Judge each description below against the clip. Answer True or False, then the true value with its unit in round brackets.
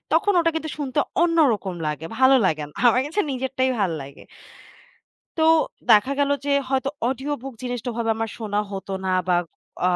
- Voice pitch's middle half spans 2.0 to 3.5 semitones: False (5.6 semitones)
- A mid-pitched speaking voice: False (250 Hz)